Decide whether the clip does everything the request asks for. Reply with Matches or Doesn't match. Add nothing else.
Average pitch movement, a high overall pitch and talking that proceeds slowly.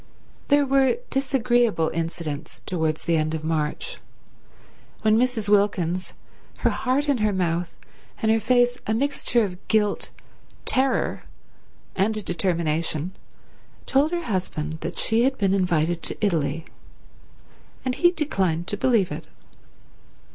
Doesn't match